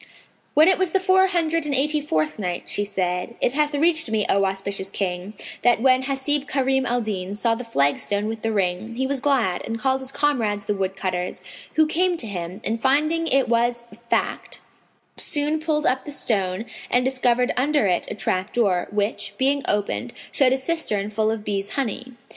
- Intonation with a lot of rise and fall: Yes, wide, 5.8 semitones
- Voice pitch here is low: No, high, 240 Hz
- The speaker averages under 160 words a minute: No, average, 190 wpm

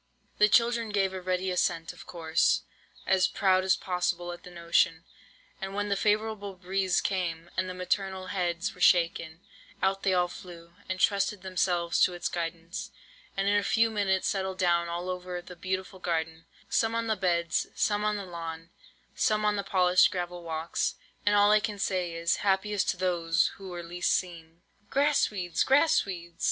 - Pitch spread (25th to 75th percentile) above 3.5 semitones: No, narrow, 2.6 semitones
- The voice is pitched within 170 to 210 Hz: Yes, medium, 185 Hz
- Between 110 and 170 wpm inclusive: No, average, 180 wpm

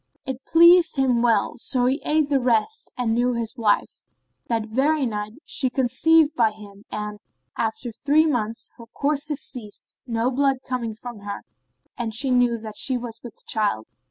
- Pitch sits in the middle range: No, high, 245 Hz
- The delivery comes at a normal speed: Yes, average, 170 wpm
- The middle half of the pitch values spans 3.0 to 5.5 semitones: Yes, average, 3.6 semitones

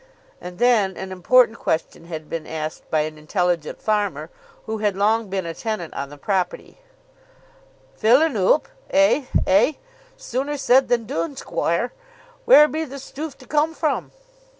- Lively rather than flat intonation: Yes, wide, 7.1 semitones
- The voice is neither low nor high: No, high, 215 Hz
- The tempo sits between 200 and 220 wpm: No, average, 155 wpm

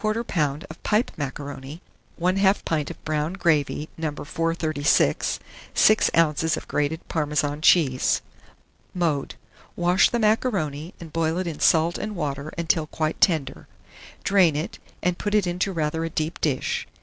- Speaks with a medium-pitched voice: Yes, medium, 160 Hz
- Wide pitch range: No, average, 3.1 semitones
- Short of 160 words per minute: Yes, average, 140 wpm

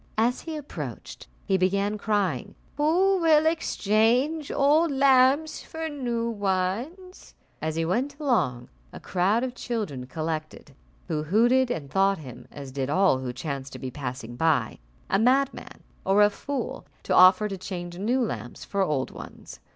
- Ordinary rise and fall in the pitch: No, wide, 9.0 semitones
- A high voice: Yes, high, 205 Hz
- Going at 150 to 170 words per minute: Yes, average, 155 wpm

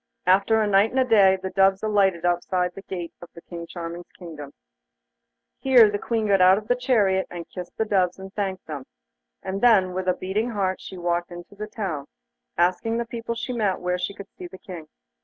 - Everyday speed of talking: No, fast, 210 wpm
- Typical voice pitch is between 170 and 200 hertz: Yes, high, 190 Hz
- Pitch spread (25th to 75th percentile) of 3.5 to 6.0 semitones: No, average, 3.1 semitones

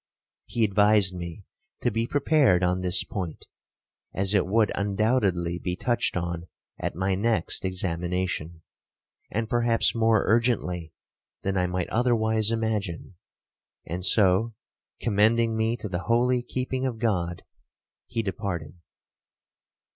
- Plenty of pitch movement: No, average, 4.2 semitones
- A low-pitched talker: Yes, low, 100 Hz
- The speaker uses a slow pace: Yes, slow, 125 wpm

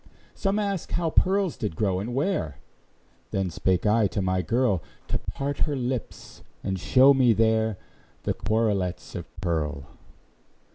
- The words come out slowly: No, average, 145 wpm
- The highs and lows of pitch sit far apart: Yes, wide, 6.4 semitones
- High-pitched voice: No, low, 110 Hz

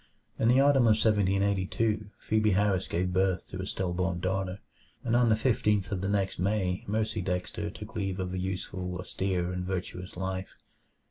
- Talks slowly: No, average, 180 wpm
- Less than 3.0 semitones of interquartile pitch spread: Yes, narrow, 2.4 semitones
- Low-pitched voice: Yes, very low, 95 Hz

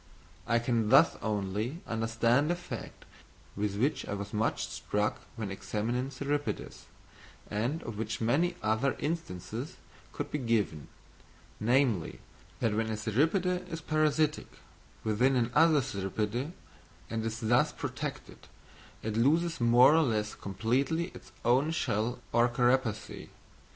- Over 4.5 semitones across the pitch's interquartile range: Yes, average, 4.9 semitones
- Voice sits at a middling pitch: No, low, 120 Hz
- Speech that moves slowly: Yes, slow, 125 wpm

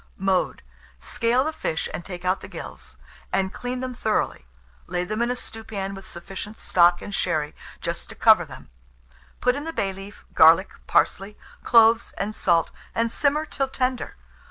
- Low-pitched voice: No, high, 205 Hz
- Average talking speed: Yes, average, 170 wpm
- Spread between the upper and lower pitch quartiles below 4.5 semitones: No, average, 5.1 semitones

